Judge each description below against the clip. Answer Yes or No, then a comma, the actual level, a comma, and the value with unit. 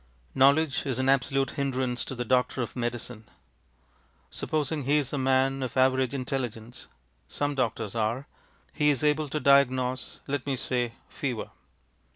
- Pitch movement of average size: No, narrow, 2.1 semitones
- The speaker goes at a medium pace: Yes, average, 150 wpm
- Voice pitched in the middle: No, low, 130 Hz